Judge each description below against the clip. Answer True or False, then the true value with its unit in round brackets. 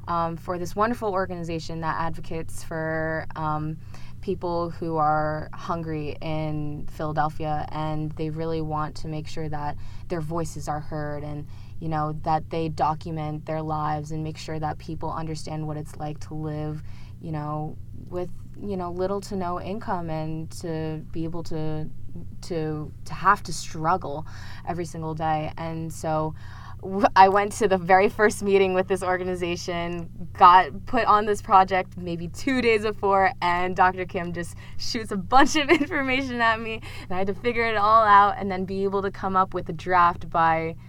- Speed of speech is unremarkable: True (175 wpm)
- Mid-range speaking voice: True (165 Hz)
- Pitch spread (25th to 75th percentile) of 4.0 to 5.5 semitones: False (3.5 semitones)